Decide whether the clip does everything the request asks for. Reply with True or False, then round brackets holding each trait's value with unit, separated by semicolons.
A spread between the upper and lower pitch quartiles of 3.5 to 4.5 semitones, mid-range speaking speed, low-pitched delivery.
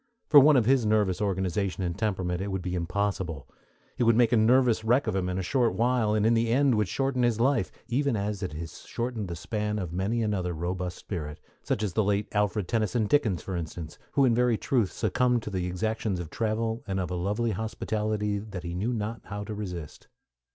False (3.9 semitones; 220 wpm; 105 Hz)